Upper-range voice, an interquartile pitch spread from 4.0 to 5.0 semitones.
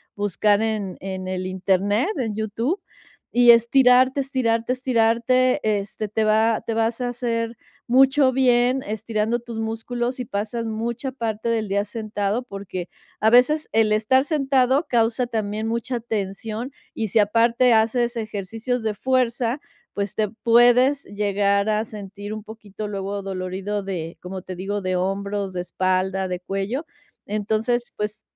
No: high, 220 Hz; average, 3.1 semitones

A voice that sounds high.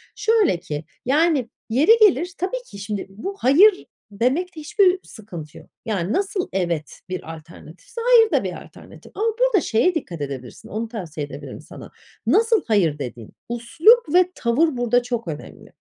Yes: high, 245 Hz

